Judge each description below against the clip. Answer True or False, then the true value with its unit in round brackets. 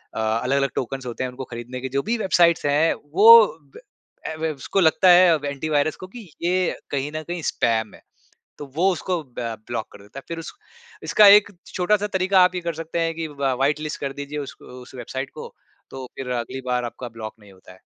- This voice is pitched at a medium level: True (145 Hz)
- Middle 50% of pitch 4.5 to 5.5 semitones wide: True (5.2 semitones)